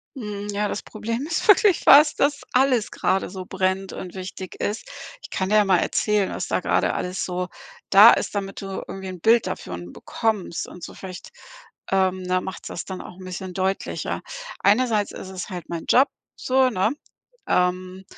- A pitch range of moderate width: Yes, average, 3.1 semitones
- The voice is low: No, high, 195 Hz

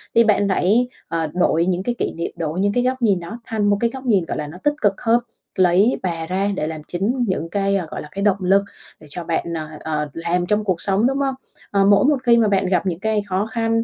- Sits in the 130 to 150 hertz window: No, high, 195 Hz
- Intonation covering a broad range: No, average, 4.4 semitones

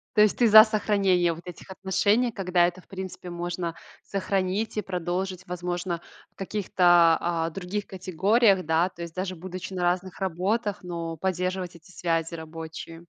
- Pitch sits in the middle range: Yes, medium, 180 Hz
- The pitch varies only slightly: Yes, narrow, 2.0 semitones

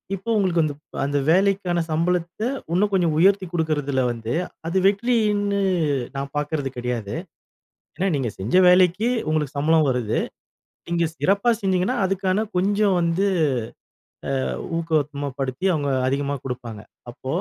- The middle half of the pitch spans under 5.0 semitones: No, wide, 5.4 semitones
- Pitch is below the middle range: No, medium, 165 Hz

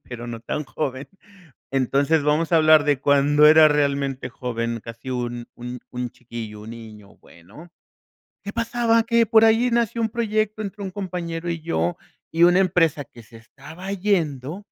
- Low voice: No, medium, 150 Hz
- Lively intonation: Yes, wide, 7.6 semitones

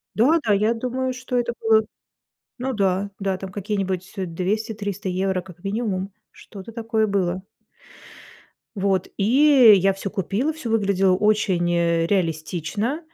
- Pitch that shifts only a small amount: No, average, 3.1 semitones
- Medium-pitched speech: No, high, 200 Hz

